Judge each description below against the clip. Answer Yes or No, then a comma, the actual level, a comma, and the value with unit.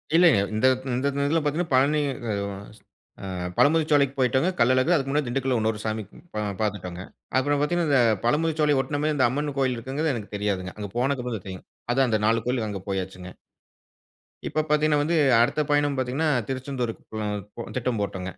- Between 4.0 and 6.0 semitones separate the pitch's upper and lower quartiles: Yes, average, 5.0 semitones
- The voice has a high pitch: No, low, 130 Hz